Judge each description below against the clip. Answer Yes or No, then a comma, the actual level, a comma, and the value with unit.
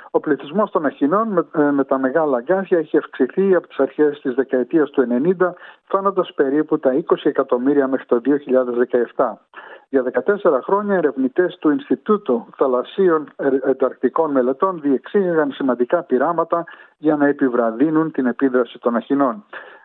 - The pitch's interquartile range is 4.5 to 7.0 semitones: Yes, average, 4.8 semitones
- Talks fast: No, average, 135 wpm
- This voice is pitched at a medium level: Yes, medium, 145 Hz